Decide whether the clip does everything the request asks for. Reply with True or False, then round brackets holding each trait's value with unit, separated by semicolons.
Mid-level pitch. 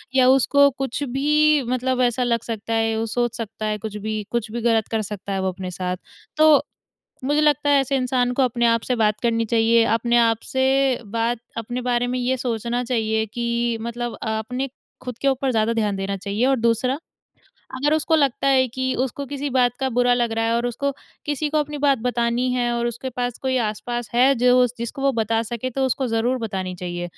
False (240 Hz)